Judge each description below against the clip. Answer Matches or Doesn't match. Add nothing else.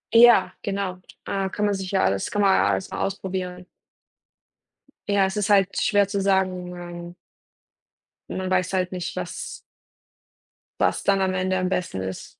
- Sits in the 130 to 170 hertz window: Doesn't match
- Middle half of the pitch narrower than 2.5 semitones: Matches